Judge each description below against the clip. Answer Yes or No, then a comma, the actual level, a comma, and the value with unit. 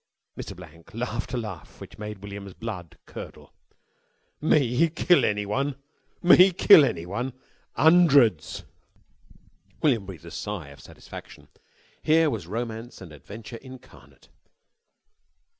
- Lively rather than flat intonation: Yes, wide, 6.0 semitones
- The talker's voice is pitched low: Yes, low, 115 Hz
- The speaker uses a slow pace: Yes, slow, 110 wpm